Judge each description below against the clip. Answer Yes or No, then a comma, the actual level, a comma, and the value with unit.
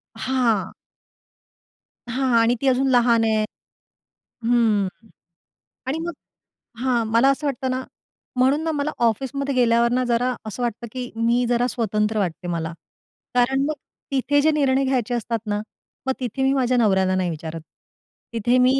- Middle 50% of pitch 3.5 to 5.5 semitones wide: No, average, 2.8 semitones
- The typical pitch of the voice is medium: No, high, 245 Hz